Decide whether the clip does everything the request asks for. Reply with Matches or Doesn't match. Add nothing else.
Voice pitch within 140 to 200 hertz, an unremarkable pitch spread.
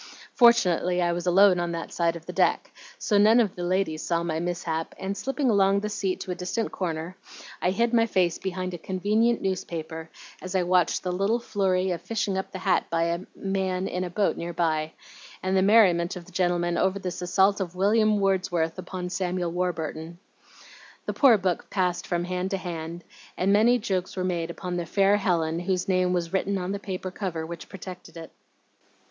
Doesn't match